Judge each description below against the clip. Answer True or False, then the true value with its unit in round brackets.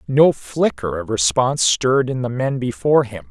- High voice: False (120 Hz)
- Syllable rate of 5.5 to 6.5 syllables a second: False (5.1 syllables/s)